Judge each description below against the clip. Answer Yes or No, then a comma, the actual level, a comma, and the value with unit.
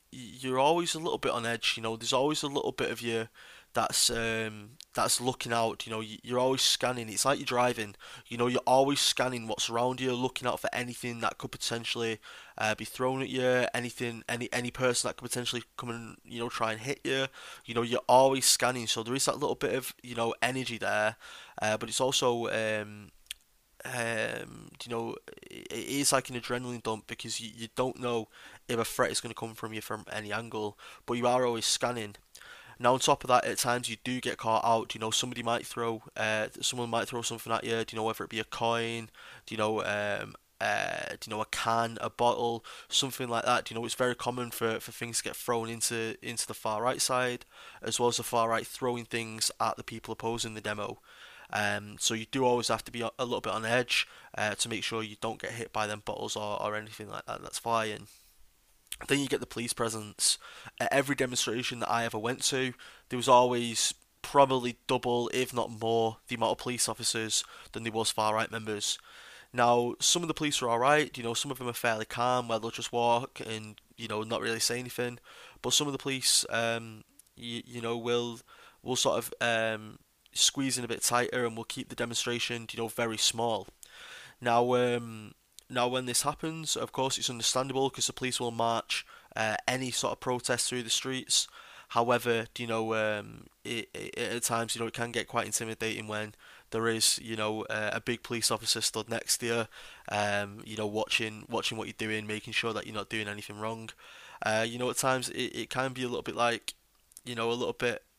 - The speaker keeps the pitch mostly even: Yes, narrow, 1.8 semitones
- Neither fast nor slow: No, fast, 225 wpm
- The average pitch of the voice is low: Yes, low, 115 Hz